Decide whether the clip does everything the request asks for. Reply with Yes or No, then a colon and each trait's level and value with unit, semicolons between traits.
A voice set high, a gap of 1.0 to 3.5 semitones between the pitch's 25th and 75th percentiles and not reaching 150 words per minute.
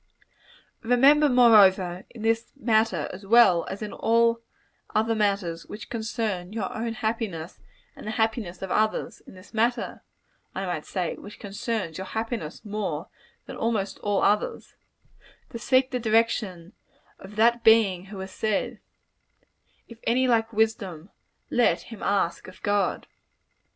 Yes: high, 215 Hz; average, 3.2 semitones; average, 140 wpm